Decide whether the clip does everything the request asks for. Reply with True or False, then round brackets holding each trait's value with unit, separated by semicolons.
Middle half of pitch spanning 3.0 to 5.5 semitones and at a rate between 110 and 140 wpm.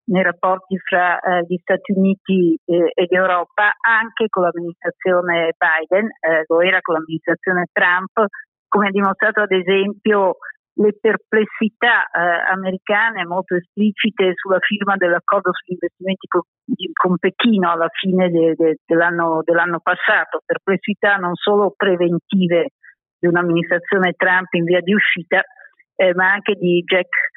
False (2.4 semitones; 135 wpm)